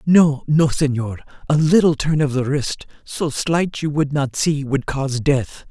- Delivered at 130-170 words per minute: No, average, 190 wpm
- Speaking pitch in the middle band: Yes, medium, 145 Hz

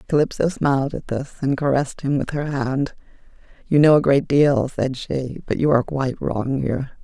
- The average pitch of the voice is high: No, low, 135 Hz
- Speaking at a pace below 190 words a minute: No, average, 195 wpm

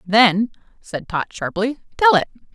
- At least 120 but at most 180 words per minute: Yes, average, 140 wpm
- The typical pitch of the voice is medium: No, high, 220 Hz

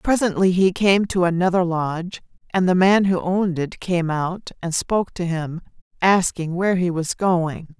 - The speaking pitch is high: No, medium, 180 Hz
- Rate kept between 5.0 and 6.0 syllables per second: No, 4.6 syllables/s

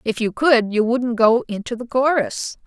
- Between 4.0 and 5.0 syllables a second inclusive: Yes, 4.4 syllables/s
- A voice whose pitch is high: Yes, high, 235 Hz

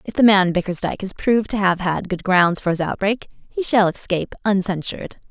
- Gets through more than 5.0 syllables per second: Yes, 5.6 syllables/s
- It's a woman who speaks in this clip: Yes, female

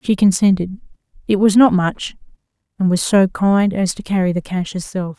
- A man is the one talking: No, female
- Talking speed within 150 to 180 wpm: Yes, average, 160 wpm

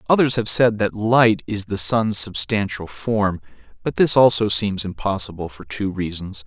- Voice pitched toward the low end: Yes, low, 105 Hz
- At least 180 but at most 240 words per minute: No, average, 165 wpm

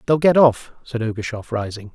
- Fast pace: No, average, 185 wpm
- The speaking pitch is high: No, low, 120 Hz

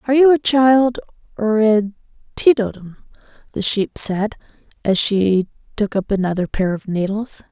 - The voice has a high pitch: Yes, high, 215 Hz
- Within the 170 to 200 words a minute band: No, average, 145 wpm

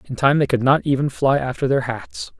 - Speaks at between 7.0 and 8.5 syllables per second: No, 5.4 syllables/s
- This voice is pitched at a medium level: No, low, 125 Hz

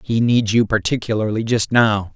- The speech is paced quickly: No, average, 165 wpm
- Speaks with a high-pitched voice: No, low, 110 Hz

